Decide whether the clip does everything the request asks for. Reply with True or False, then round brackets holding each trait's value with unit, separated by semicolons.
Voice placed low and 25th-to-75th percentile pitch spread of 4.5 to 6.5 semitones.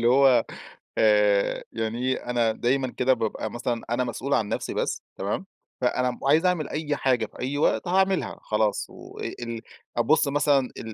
False (125 Hz; 3.7 semitones)